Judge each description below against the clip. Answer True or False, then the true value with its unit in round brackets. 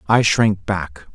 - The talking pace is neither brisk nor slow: True (155 wpm)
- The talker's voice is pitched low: True (100 Hz)